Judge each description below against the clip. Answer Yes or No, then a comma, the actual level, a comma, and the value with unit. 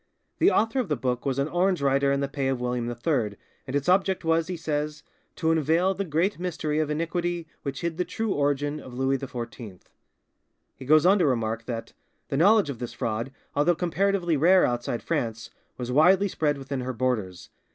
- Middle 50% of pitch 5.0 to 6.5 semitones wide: Yes, average, 5.3 semitones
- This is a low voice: No, medium, 145 Hz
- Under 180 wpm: No, average, 195 wpm